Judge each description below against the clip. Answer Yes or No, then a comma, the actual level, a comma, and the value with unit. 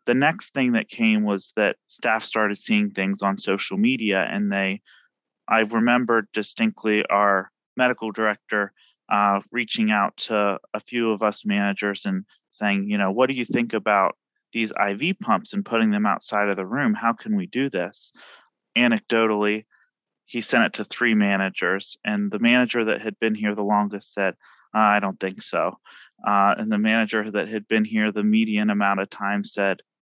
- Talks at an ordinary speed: Yes, average, 180 wpm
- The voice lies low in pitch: Yes, low, 110 Hz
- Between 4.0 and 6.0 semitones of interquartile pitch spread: No, average, 3.1 semitones